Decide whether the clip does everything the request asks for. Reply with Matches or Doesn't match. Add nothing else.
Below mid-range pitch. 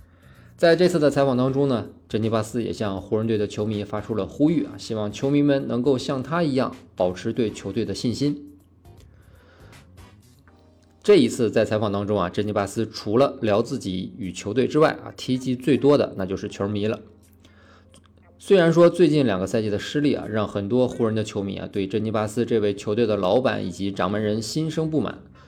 Matches